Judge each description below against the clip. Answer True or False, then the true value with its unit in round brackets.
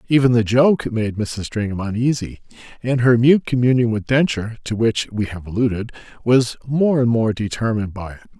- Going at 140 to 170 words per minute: False (180 wpm)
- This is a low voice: True (115 Hz)